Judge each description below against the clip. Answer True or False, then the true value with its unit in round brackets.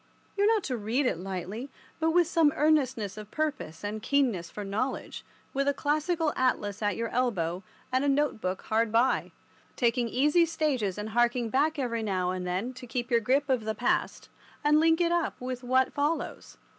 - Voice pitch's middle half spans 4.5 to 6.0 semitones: True (5.5 semitones)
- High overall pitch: True (250 Hz)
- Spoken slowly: False (195 wpm)